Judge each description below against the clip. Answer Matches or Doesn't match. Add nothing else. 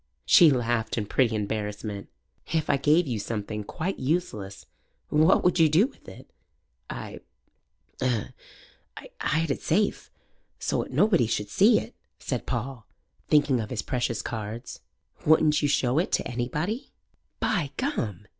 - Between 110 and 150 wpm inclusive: Matches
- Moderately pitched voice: Doesn't match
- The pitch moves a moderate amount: Doesn't match